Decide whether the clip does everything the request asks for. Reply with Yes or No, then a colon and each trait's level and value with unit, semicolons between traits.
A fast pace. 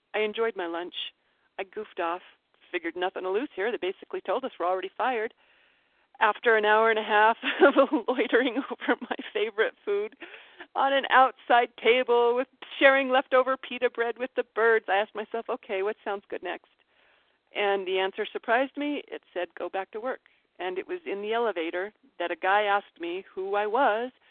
No: average, 190 wpm